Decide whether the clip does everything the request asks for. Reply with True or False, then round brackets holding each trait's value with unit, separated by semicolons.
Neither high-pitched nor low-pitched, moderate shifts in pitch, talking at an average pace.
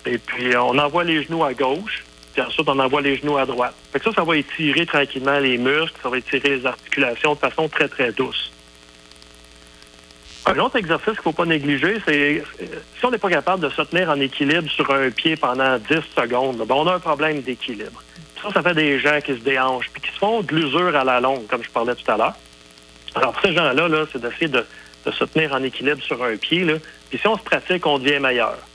False (145 Hz; 4.0 semitones; 235 wpm)